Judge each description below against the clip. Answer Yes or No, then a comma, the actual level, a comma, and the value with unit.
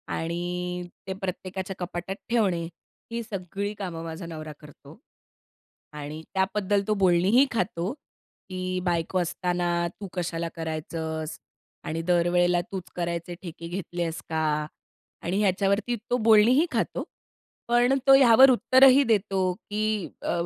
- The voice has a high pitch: No, medium, 180 Hz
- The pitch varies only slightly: No, average, 3.5 semitones